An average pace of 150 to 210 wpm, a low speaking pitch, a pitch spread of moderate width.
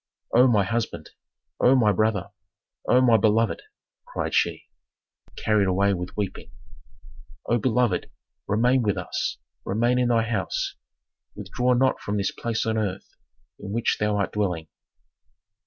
No: average, 140 wpm; low, 110 Hz; average, 3.1 semitones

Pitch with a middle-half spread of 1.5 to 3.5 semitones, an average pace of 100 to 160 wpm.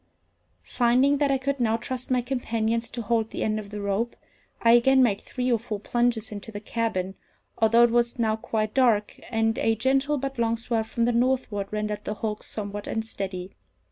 No: narrow, 2.4 semitones; average, 195 wpm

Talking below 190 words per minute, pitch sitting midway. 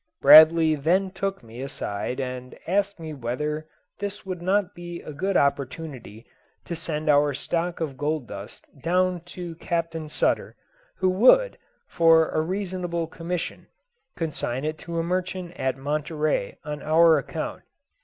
Yes: average, 145 wpm; medium, 160 Hz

